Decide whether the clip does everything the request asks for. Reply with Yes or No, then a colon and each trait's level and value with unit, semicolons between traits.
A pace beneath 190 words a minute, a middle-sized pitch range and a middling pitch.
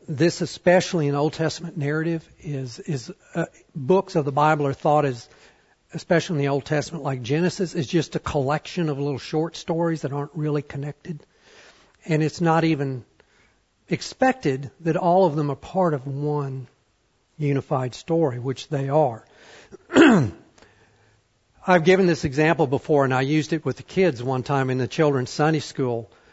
Yes: average, 165 wpm; average, 3.3 semitones; medium, 150 Hz